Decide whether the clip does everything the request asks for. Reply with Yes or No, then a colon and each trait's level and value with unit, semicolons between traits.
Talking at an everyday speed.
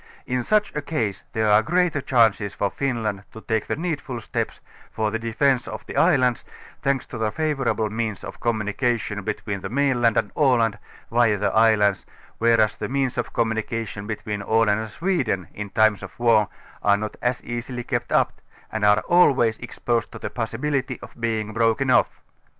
Yes: average, 175 wpm